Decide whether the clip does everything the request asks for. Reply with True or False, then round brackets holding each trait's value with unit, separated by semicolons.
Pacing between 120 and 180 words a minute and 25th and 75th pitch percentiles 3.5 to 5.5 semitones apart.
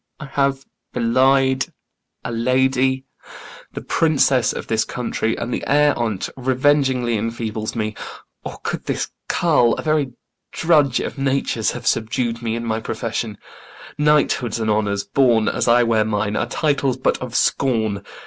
False (150 wpm; 3.1 semitones)